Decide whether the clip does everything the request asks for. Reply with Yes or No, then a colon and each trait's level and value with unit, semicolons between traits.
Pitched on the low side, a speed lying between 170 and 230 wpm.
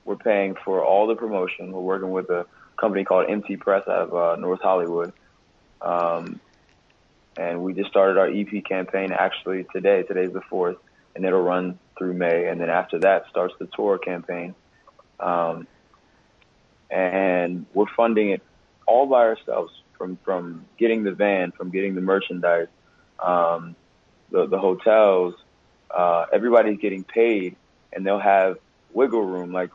No: very low, 95 Hz; average, 155 wpm